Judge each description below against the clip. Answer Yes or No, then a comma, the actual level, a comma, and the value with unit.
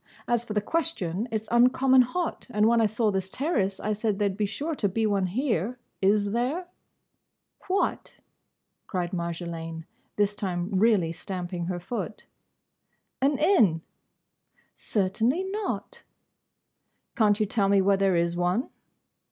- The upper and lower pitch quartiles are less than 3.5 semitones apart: No, average, 4.4 semitones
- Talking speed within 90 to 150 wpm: Yes, average, 145 wpm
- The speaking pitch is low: No, high, 210 Hz